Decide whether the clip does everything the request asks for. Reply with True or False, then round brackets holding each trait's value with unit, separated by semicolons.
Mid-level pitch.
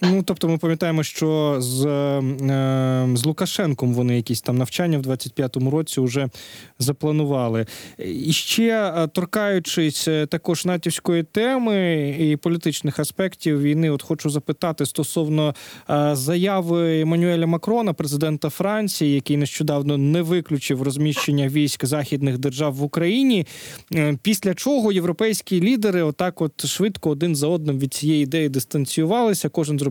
True (155 Hz)